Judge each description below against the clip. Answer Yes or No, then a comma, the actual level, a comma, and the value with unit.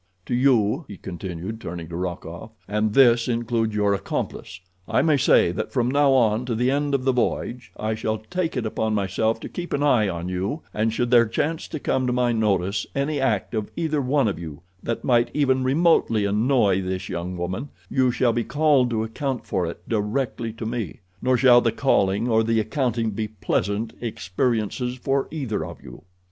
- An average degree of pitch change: Yes, average, 4.1 semitones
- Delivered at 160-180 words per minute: No, average, 195 wpm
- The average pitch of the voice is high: No, low, 115 Hz